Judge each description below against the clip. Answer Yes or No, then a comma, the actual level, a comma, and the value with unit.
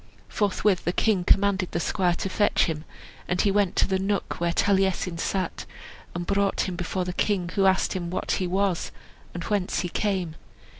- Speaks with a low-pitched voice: No, high, 190 Hz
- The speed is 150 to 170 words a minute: No, average, 190 wpm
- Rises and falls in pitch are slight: Yes, narrow, 2.0 semitones